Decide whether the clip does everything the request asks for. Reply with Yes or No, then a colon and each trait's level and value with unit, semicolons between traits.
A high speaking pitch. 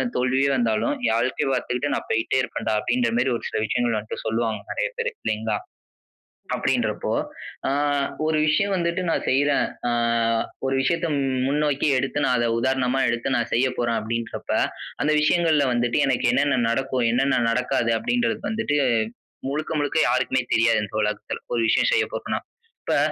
No: low, 130 Hz